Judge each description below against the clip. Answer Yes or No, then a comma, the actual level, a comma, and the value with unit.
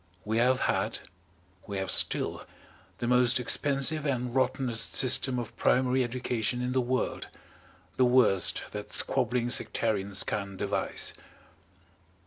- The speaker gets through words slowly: Yes, slow, 120 wpm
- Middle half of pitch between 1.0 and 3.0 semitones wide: Yes, narrow, 2.6 semitones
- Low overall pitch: Yes, low, 125 Hz